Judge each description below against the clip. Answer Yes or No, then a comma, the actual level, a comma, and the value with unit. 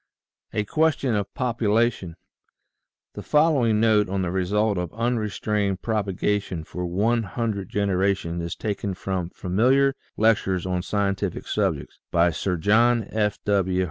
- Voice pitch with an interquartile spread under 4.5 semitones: Yes, average, 3.3 semitones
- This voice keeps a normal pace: No, slow, 130 wpm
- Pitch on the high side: No, low, 100 Hz